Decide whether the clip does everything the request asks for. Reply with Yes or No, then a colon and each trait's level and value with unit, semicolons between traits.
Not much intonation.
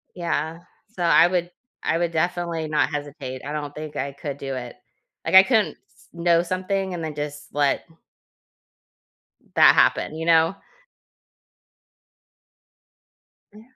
No: average, 3.0 semitones